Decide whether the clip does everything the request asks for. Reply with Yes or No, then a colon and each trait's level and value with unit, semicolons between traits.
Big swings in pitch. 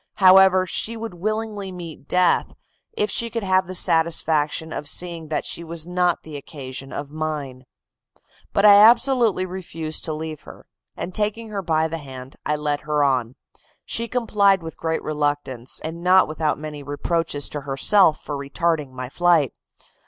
No: average, 4.2 semitones